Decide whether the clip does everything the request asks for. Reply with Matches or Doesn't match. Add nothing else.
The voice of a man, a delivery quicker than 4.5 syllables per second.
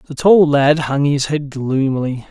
Doesn't match